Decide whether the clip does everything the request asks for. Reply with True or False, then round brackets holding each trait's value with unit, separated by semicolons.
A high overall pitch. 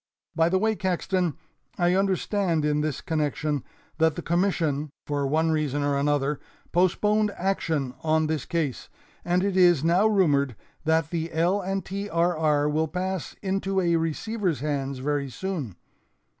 False (165 Hz)